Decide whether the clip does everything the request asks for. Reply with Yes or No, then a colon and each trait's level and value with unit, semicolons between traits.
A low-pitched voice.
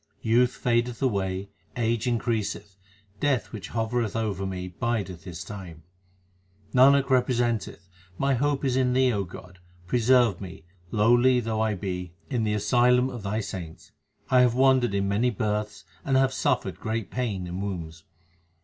Yes: low, 110 Hz